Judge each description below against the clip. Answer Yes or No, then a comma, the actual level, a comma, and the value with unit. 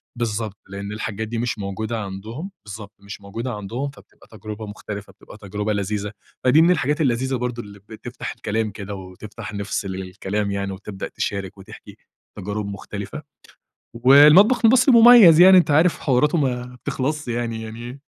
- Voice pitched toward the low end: Yes, low, 110 Hz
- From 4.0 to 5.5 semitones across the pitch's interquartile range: Yes, average, 4.7 semitones